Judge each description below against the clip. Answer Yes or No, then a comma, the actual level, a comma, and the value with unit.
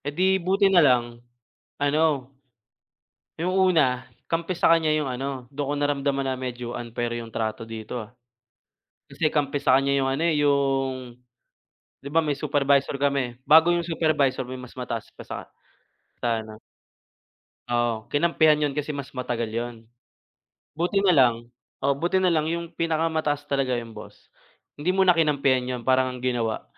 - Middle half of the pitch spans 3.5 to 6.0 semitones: Yes, average, 4.1 semitones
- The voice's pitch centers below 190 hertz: Yes, medium, 140 Hz